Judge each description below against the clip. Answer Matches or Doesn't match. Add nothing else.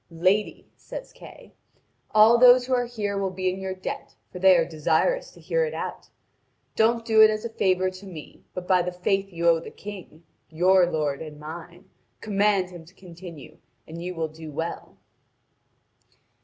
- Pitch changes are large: Doesn't match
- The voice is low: Doesn't match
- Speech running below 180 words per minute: Doesn't match